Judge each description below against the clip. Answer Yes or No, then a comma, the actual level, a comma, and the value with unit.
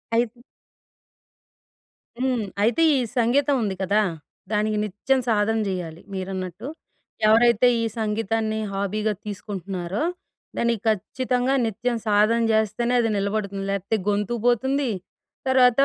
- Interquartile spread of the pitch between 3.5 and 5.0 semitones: No, average, 3.0 semitones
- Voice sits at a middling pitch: No, high, 220 Hz